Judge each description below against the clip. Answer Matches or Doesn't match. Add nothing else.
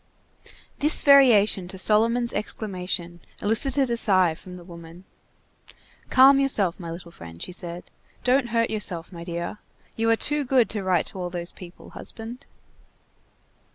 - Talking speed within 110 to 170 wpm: Matches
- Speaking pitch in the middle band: Doesn't match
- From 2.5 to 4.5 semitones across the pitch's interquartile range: Doesn't match